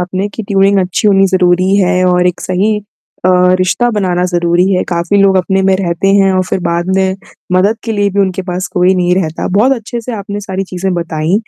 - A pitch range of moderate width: No, narrow, 1.9 semitones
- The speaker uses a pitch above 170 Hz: Yes, high, 190 Hz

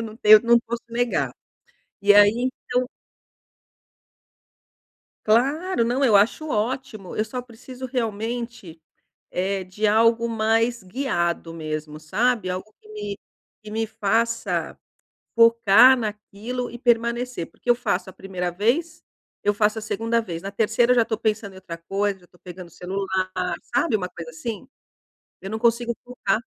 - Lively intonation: No, average, 3.6 semitones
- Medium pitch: No, high, 220 Hz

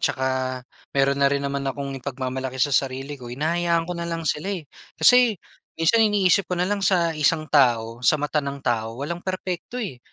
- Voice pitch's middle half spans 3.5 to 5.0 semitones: Yes, average, 4.4 semitones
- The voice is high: No, medium, 150 Hz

